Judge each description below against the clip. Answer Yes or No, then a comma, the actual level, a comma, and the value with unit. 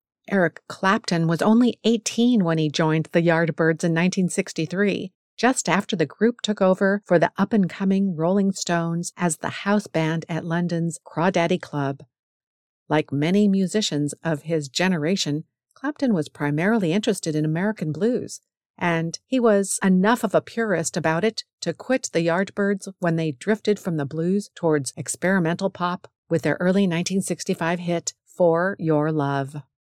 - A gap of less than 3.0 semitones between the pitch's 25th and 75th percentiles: No, average, 3.7 semitones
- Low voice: No, medium, 175 Hz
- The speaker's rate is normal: Yes, average, 155 wpm